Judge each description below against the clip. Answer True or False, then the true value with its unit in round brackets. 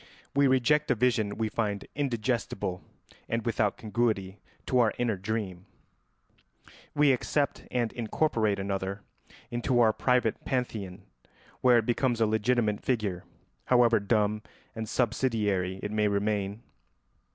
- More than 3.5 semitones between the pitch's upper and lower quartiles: False (3.0 semitones)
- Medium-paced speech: False (125 wpm)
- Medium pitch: False (110 Hz)